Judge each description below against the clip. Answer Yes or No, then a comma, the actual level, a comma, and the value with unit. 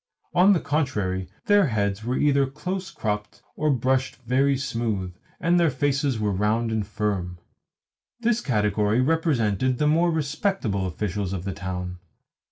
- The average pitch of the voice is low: Yes, low, 120 Hz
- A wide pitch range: Yes, wide, 6.5 semitones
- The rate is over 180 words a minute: No, average, 145 wpm